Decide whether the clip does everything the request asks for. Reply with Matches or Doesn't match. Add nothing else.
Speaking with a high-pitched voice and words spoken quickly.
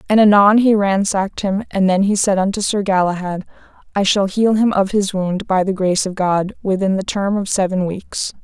Matches